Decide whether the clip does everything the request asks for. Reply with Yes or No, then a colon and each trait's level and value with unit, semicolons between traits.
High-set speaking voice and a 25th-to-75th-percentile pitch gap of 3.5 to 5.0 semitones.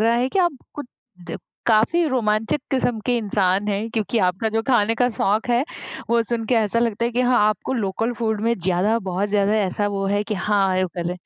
No: high, 220 Hz; average, 2.8 semitones